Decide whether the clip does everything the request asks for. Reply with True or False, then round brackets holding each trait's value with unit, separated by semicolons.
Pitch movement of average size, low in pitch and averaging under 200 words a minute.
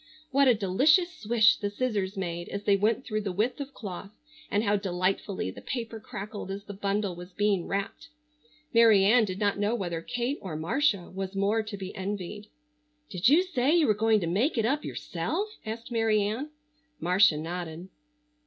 False (3.3 semitones; 205 Hz; 185 wpm)